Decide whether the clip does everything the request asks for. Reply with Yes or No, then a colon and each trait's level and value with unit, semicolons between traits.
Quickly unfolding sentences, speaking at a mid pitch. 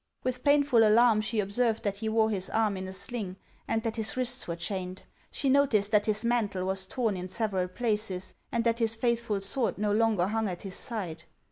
No: fast, 210 wpm; high, 215 Hz